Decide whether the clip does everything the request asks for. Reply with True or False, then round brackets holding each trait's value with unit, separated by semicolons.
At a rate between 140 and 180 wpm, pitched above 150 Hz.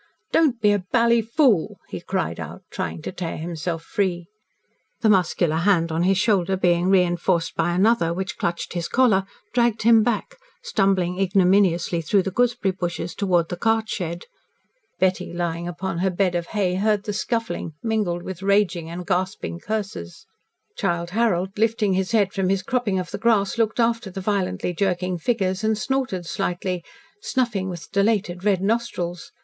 True (165 wpm; 190 Hz)